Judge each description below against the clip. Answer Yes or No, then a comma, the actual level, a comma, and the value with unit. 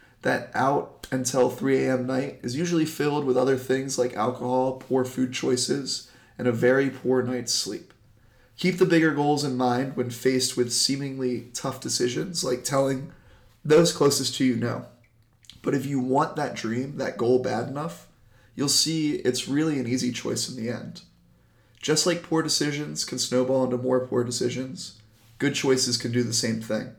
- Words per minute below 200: Yes, average, 175 wpm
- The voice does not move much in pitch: Yes, narrow, 2.1 semitones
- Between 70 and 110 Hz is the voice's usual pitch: No, low, 130 Hz